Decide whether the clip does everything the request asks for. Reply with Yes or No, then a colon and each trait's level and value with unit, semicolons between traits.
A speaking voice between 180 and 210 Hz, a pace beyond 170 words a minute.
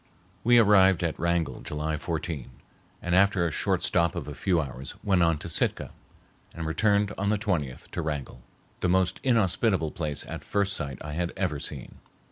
No: very low, 85 Hz; average, 185 wpm